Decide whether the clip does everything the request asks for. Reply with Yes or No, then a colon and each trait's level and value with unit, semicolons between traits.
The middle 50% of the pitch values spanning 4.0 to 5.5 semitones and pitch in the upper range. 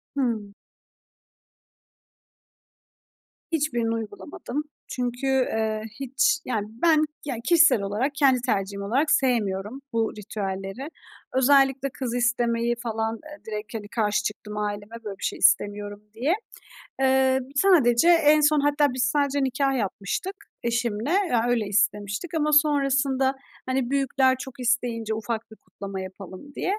Yes: average, 4.4 semitones; high, 245 Hz